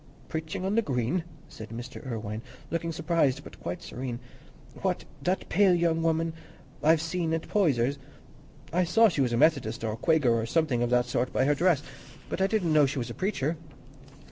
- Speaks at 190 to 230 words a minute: Yes, average, 195 wpm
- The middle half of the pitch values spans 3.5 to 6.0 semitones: Yes, wide, 5.6 semitones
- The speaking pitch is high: No, medium, 155 Hz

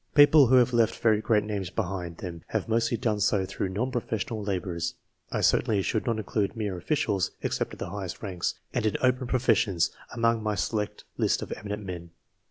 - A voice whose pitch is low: Yes, low, 105 Hz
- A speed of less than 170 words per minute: No, average, 190 wpm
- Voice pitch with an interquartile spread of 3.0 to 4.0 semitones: Yes, average, 3.5 semitones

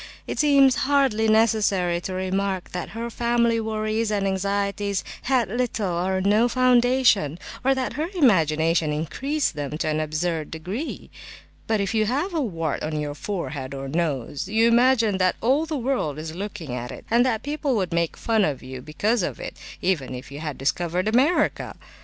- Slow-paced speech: No, average, 175 wpm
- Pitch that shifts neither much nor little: No, wide, 6.7 semitones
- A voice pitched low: No, high, 200 Hz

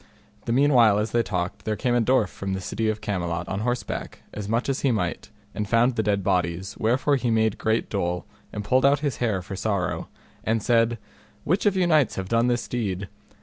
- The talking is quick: Yes, fast, 215 wpm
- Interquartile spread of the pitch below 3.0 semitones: No, average, 3.7 semitones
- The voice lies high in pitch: No, low, 110 Hz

